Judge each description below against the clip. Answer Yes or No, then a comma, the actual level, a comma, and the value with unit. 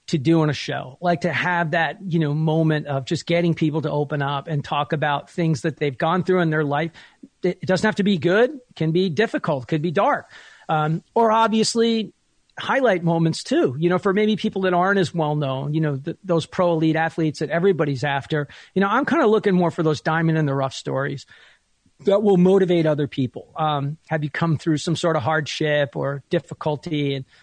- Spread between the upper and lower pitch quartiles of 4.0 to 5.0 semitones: No, average, 3.3 semitones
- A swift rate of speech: Yes, fast, 220 wpm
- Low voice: No, medium, 165 Hz